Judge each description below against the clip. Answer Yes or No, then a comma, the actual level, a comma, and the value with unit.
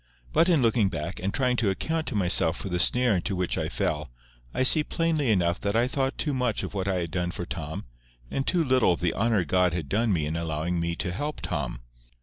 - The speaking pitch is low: Yes, very low, 95 Hz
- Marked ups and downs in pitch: Yes, wide, 6.5 semitones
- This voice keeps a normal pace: No, fast, 240 wpm